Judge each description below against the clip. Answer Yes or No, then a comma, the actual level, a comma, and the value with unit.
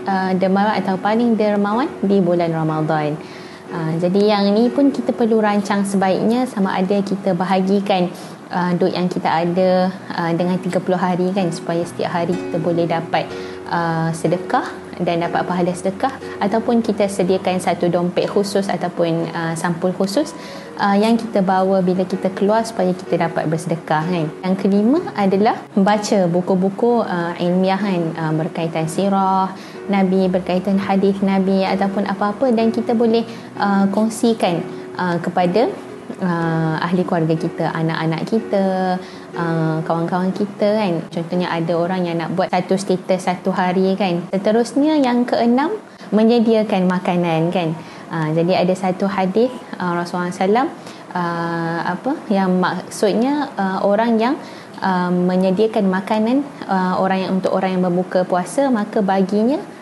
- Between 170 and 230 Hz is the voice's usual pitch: Yes, high, 190 Hz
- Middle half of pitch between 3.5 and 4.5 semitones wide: No, average, 2.8 semitones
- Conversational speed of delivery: Yes, average, 145 wpm